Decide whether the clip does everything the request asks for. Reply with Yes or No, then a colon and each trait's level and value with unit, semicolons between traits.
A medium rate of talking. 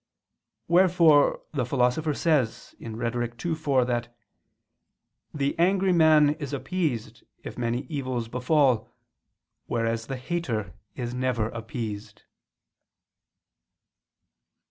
No: slow, 95 wpm